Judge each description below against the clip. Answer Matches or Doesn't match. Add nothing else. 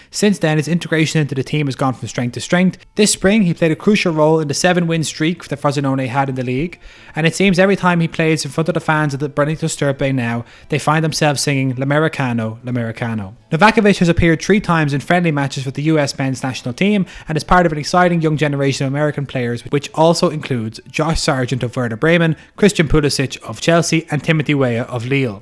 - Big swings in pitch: Doesn't match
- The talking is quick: Matches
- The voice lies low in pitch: Doesn't match